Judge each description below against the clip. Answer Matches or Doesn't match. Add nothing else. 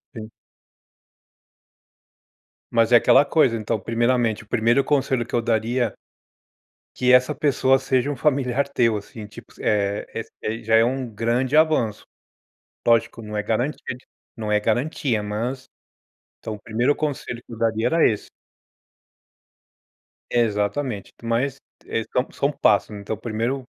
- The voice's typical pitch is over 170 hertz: Doesn't match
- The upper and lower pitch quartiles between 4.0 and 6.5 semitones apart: Doesn't match